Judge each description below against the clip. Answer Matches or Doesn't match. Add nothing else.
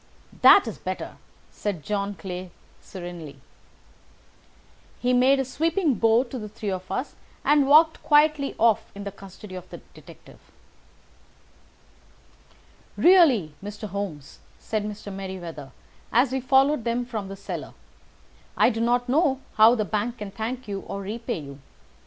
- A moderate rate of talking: Matches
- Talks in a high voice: Matches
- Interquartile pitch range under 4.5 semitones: Doesn't match